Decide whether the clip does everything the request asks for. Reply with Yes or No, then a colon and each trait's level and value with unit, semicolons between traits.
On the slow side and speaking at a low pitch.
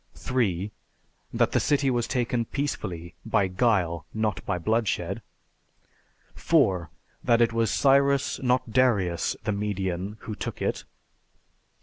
Yes: slow, 120 wpm; low, 110 Hz